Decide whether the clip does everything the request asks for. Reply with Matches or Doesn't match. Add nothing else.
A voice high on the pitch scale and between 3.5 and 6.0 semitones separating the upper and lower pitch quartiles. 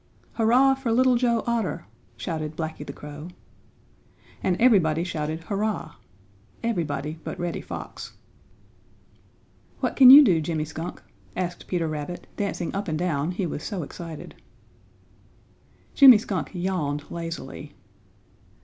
Doesn't match